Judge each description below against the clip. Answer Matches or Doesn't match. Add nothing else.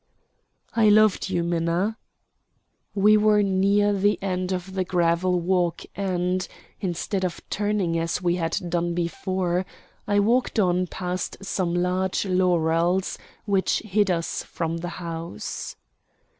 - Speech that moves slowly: Matches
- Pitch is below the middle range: Doesn't match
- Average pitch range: Doesn't match